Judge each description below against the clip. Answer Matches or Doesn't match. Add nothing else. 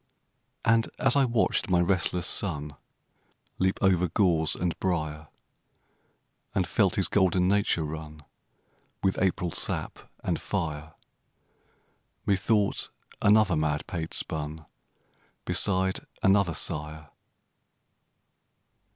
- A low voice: Matches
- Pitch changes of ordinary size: Matches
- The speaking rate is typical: Doesn't match